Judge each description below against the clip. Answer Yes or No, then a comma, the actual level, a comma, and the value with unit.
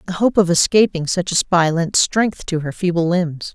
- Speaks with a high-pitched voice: No, medium, 175 Hz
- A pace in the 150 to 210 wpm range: No, fast, 220 wpm